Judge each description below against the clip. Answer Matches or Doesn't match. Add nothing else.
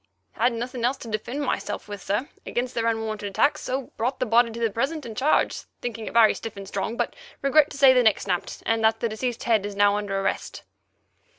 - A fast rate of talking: Matches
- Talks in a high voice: Matches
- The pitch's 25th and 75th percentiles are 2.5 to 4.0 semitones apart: Matches